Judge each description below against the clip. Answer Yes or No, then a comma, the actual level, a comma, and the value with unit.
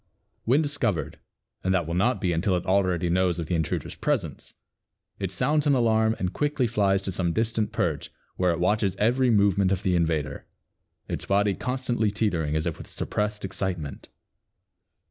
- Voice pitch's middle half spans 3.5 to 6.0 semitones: Yes, average, 4.3 semitones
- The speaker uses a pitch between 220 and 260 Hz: No, low, 100 Hz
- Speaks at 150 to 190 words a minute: Yes, average, 170 wpm